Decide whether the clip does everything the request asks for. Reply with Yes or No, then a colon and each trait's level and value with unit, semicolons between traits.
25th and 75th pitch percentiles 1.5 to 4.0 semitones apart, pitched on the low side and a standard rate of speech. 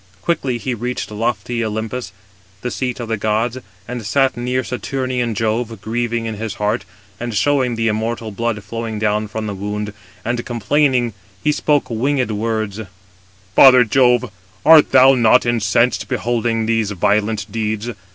Yes: narrow, 2.4 semitones; low, 115 Hz; average, 150 wpm